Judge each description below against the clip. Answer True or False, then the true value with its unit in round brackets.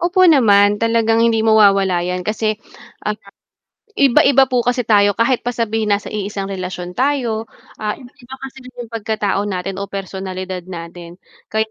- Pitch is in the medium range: False (215 Hz)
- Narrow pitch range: False (3.4 semitones)